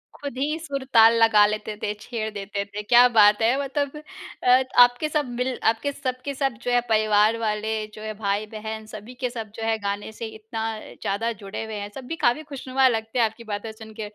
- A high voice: Yes, high, 225 Hz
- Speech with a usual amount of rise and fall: Yes, average, 3.0 semitones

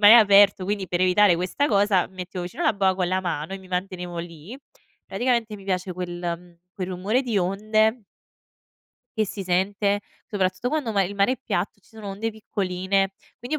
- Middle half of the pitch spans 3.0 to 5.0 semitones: No, narrow, 2.6 semitones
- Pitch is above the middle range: Yes, high, 195 Hz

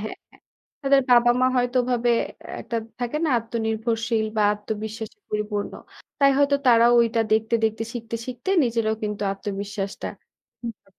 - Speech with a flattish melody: Yes, narrow, 2.0 semitones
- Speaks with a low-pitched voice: No, high, 230 Hz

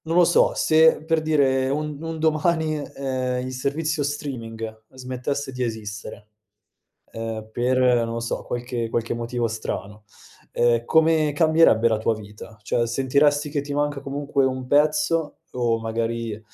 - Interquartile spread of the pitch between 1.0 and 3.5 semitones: No, average, 4.3 semitones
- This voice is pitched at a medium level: No, low, 130 Hz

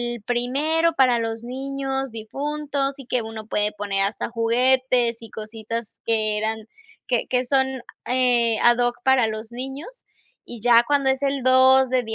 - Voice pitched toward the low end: No, high, 245 Hz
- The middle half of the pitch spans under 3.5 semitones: Yes, average, 2.9 semitones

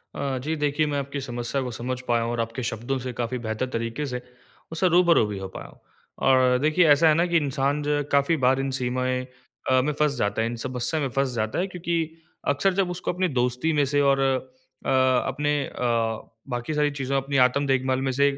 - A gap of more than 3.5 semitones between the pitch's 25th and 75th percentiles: No, average, 2.9 semitones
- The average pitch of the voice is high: No, low, 135 Hz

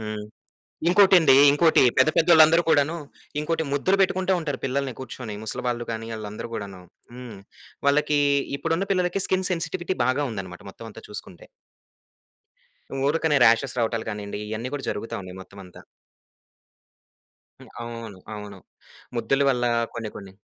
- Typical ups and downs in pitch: No, wide, 7.0 semitones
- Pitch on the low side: Yes, low, 125 Hz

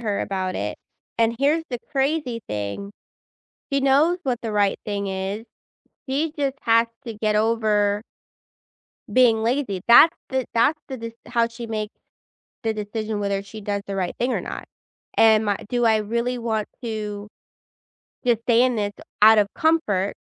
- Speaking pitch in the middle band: No, high, 225 Hz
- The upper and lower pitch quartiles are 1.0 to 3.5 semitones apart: Yes, average, 3.1 semitones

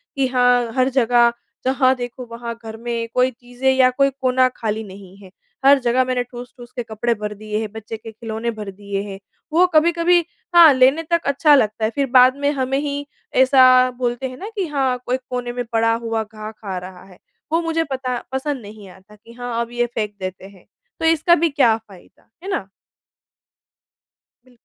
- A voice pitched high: Yes, high, 245 Hz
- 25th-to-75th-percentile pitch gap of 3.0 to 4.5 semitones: Yes, average, 3.4 semitones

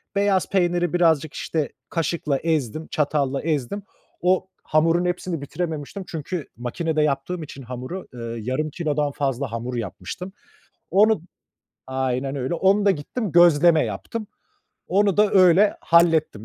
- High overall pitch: No, medium, 160 Hz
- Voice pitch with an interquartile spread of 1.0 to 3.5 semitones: No, average, 4.6 semitones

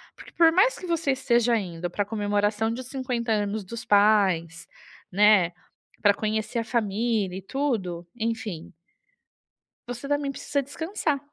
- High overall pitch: Yes, high, 220 Hz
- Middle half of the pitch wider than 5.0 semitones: No, average, 4.2 semitones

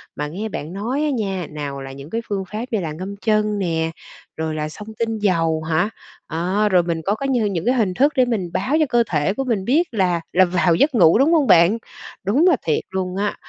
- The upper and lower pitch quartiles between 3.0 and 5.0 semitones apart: No, wide, 5.4 semitones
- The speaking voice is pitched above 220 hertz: No, high, 195 Hz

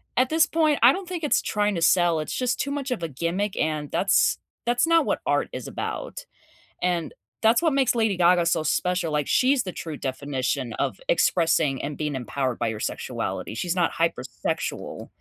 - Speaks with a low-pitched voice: No, medium, 175 Hz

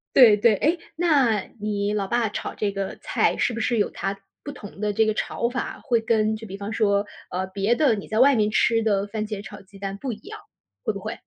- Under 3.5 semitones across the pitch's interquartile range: Yes, narrow, 2.6 semitones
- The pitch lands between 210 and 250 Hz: Yes, high, 215 Hz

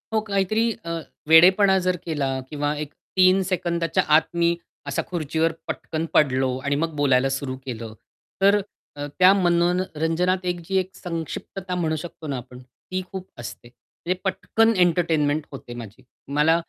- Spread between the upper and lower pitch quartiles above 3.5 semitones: Yes, average, 4.2 semitones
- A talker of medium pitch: Yes, medium, 165 Hz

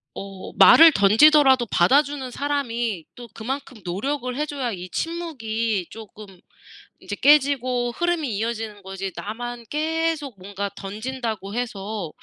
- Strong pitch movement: Yes, wide, 5.7 semitones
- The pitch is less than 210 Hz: No, high, 240 Hz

